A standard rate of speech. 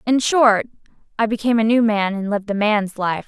No: fast, 220 wpm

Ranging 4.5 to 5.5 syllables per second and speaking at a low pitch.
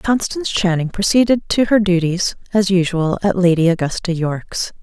No: 5.1 syllables/s; medium, 185 Hz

